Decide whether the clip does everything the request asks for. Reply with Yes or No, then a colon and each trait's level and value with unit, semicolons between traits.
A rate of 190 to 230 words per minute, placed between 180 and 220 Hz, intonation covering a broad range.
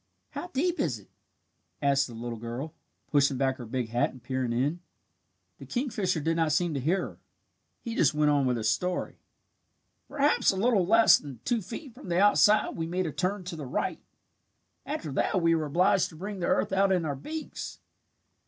No: average, 200 wpm; medium, 165 Hz; wide, 6.3 semitones